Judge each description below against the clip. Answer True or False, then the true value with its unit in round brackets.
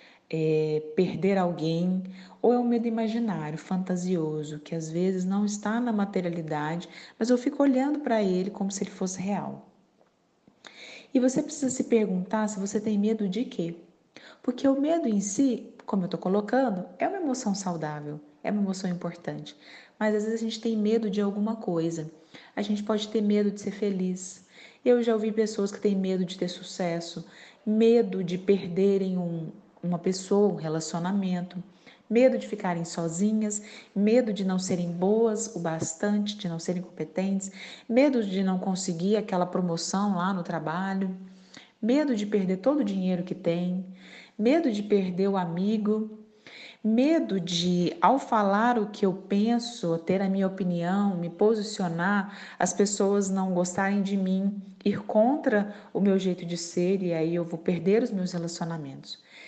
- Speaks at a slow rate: False (165 wpm)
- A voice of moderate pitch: False (195 Hz)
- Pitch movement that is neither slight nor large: True (3.3 semitones)